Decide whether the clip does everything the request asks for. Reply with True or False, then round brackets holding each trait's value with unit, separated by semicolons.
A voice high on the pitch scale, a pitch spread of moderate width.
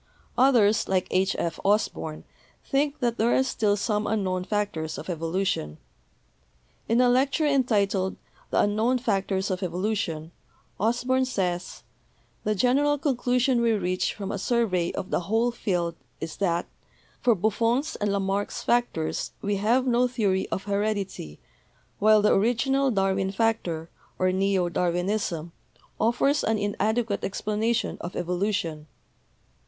True (205 Hz; 4.3 semitones)